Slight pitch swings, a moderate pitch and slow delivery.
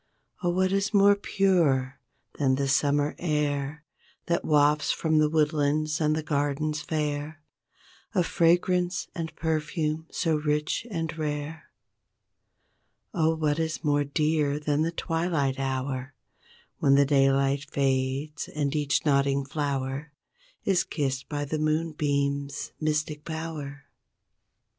Yes: narrow, 2.2 semitones; medium, 150 Hz; slow, 120 wpm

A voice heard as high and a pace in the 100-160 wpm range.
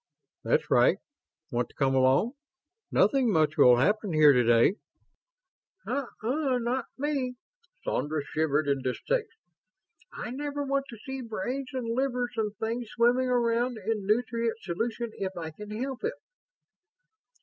Yes: high, 230 Hz; average, 140 wpm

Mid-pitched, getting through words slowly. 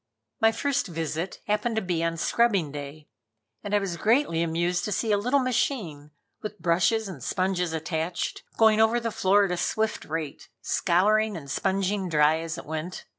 No: medium, 180 Hz; average, 180 wpm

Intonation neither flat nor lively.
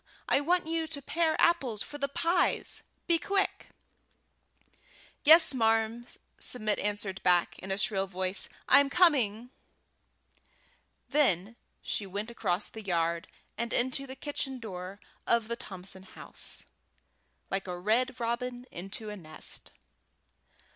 No: wide, 6.3 semitones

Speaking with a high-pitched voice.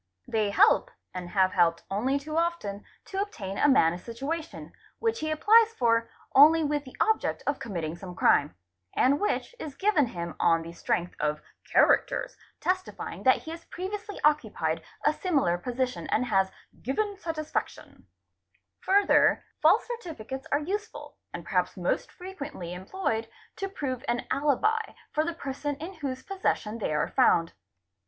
Yes: very high, 280 Hz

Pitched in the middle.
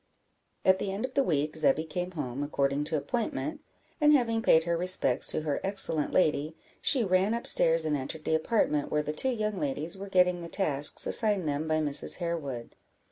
Yes: medium, 165 Hz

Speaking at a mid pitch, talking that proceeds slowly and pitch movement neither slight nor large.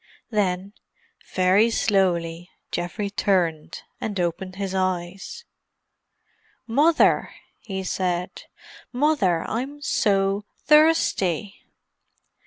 No: high, 195 Hz; slow, 75 wpm; average, 3.6 semitones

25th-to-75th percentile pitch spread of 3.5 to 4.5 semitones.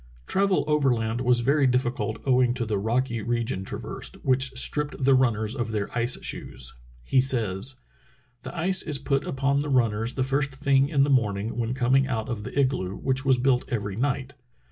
No: average, 3.0 semitones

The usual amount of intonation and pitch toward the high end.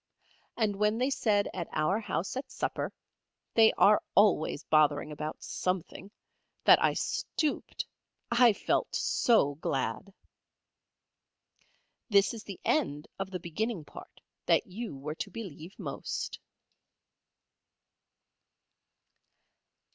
No: wide, 6.1 semitones; high, 195 Hz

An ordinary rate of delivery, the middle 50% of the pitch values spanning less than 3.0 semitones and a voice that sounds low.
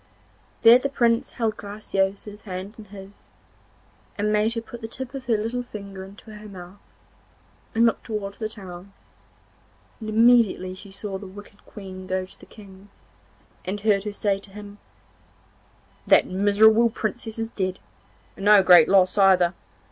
No: average, 160 wpm; narrow, 2.4 semitones; high, 205 Hz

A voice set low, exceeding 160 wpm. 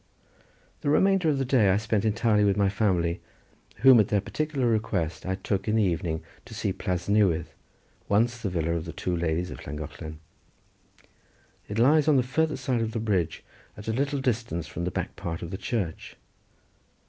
Yes: low, 105 Hz; average, 190 wpm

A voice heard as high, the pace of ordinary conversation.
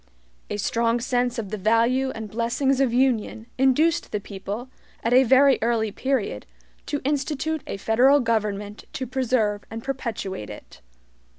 Yes: high, 235 Hz; average, 150 wpm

